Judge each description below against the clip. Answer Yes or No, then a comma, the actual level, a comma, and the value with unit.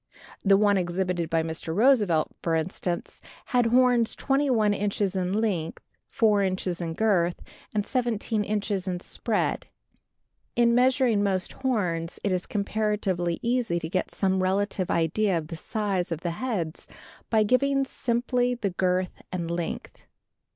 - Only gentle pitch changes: No, average, 4.4 semitones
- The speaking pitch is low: No, high, 200 Hz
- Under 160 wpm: Yes, average, 145 wpm